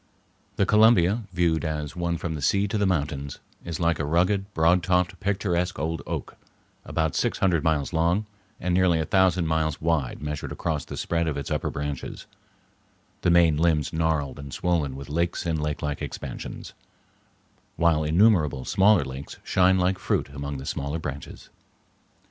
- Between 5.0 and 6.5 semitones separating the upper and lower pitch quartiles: No, average, 3.2 semitones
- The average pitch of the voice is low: Yes, very low, 80 Hz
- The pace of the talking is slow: No, average, 165 wpm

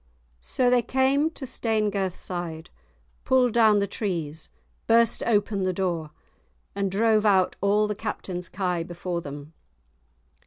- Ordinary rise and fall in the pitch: Yes, average, 4.2 semitones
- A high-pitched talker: Yes, high, 200 Hz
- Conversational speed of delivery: No, slow, 125 wpm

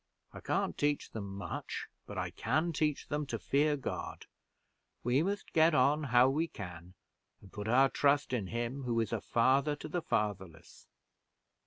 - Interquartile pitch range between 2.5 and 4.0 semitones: No, average, 5.2 semitones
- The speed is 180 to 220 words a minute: No, average, 170 wpm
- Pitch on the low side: Yes, low, 130 Hz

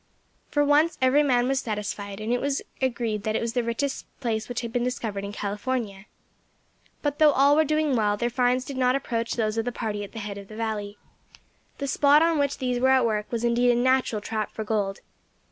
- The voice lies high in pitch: Yes, high, 240 Hz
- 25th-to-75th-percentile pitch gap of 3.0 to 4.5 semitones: Yes, average, 3.5 semitones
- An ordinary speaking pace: No, fast, 225 wpm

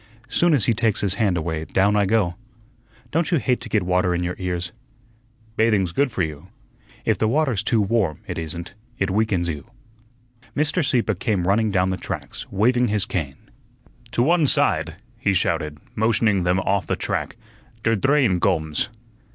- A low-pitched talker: Yes, low, 100 Hz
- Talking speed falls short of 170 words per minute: No, average, 175 wpm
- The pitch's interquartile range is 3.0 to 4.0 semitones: No, average, 4.5 semitones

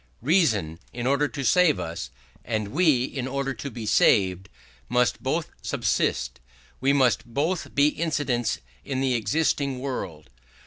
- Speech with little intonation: No, average, 4.4 semitones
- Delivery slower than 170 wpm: Yes, average, 140 wpm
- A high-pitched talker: No, low, 130 Hz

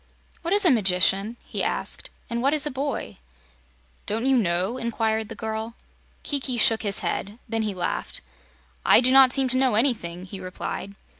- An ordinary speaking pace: Yes, average, 175 wpm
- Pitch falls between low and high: No, high, 225 Hz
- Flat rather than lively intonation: No, average, 4.4 semitones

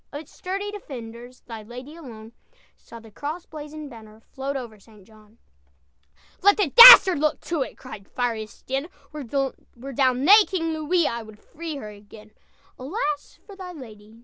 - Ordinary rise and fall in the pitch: No, wide, 6.0 semitones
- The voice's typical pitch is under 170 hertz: No, very high, 270 Hz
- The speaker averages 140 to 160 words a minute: Yes, average, 155 wpm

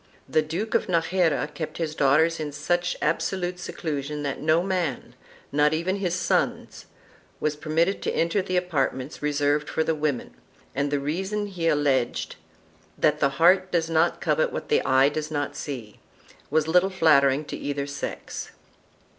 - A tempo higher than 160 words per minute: Yes, average, 170 wpm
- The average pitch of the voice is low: No, medium, 155 Hz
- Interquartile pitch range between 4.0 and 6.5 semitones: No, average, 3.3 semitones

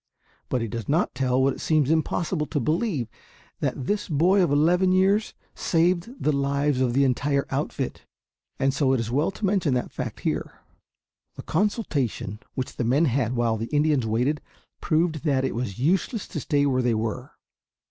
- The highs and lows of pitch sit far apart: No, average, 4.7 semitones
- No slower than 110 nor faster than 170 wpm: No, average, 180 wpm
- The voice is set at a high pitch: No, medium, 140 Hz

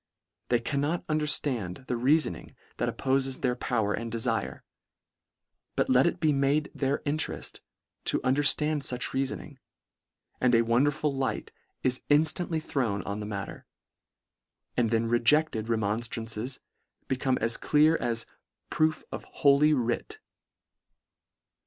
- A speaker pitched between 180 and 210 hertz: No, low, 130 Hz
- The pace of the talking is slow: Yes, slow, 130 wpm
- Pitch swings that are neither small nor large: Yes, average, 4.3 semitones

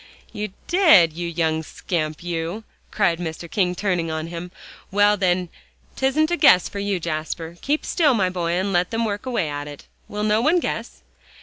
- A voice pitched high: No, medium, 180 Hz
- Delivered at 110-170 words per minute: No, average, 185 wpm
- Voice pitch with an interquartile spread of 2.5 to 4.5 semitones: Yes, average, 4.1 semitones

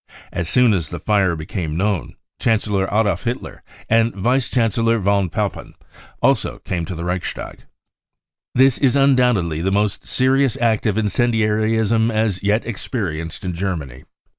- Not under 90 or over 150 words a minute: No, average, 160 wpm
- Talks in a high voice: No, low, 105 Hz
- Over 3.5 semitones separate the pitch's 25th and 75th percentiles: Yes, average, 4.2 semitones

